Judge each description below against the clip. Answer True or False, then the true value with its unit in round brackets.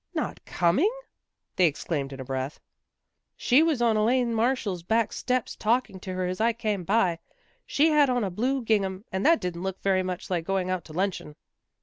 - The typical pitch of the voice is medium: False (195 Hz)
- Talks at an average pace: False (215 wpm)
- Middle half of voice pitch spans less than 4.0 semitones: False (4.8 semitones)